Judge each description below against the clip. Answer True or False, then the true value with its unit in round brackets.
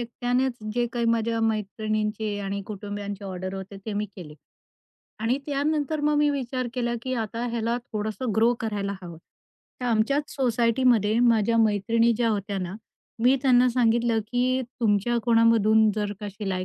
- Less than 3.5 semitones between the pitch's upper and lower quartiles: True (2.9 semitones)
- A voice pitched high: True (225 Hz)